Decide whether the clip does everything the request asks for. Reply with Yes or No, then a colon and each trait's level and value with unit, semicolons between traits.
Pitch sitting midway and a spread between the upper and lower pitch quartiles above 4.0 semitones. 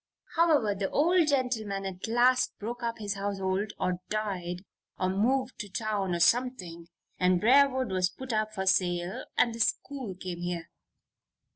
No: high, 205 Hz; average, 5.1 semitones